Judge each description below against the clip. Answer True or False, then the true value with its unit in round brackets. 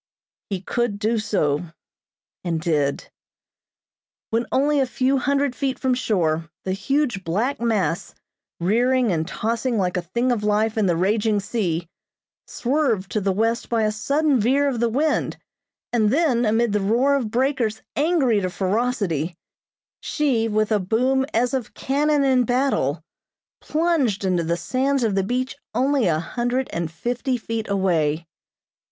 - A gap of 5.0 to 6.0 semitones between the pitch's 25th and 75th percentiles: True (5.3 semitones)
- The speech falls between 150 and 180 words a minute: True (155 wpm)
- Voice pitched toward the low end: False (225 Hz)